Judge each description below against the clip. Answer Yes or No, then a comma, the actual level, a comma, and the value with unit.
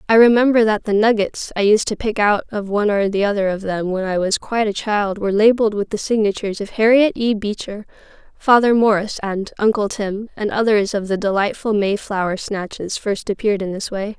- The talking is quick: Yes, fast, 210 wpm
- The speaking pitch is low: No, high, 210 Hz